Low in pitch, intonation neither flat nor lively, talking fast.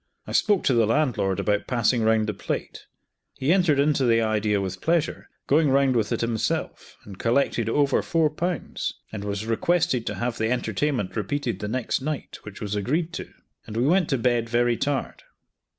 No: low, 120 Hz; average, 5.0 semitones; average, 185 wpm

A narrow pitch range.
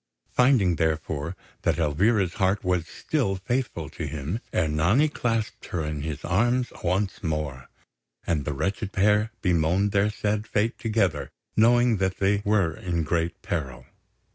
No: average, 4.8 semitones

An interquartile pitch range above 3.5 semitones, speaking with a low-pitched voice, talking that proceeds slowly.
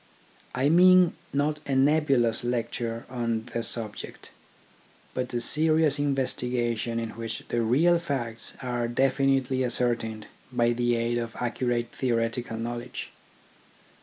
No: average, 2.7 semitones; low, 120 Hz; slow, 120 wpm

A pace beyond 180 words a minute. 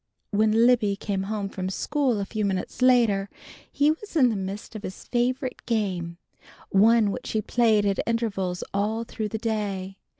No: average, 170 wpm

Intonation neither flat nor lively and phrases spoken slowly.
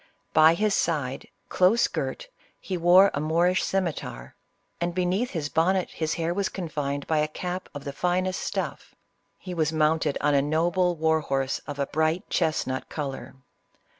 No: average, 3.5 semitones; average, 165 wpm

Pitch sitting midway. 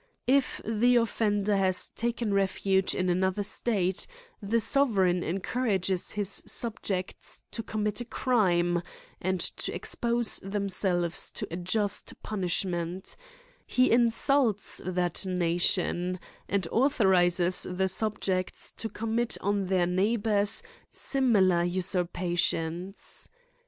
No: high, 195 Hz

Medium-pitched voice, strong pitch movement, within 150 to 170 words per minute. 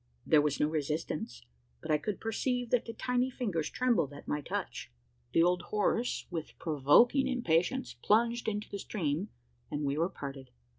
Yes: medium, 180 Hz; wide, 7.8 semitones; average, 165 wpm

